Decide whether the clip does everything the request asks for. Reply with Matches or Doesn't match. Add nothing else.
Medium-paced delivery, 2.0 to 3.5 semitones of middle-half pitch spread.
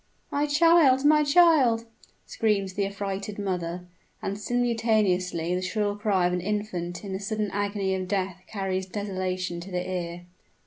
Matches